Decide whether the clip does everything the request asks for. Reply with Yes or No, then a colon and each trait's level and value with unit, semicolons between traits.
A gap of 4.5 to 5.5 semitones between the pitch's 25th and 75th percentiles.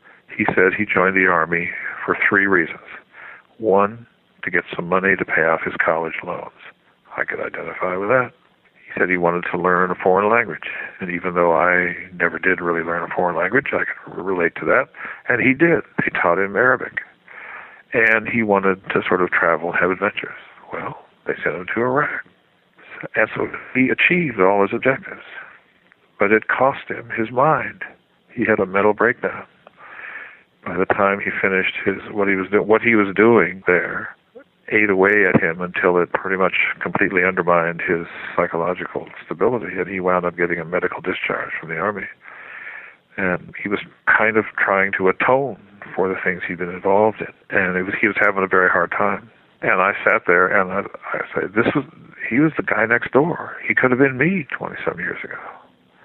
No: average, 3.5 semitones